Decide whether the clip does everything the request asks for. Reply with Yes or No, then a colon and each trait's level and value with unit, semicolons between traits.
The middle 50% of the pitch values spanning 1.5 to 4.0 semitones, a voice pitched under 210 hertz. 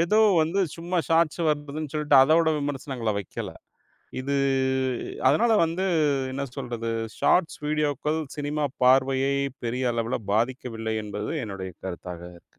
No: average, 5.0 semitones; low, 135 Hz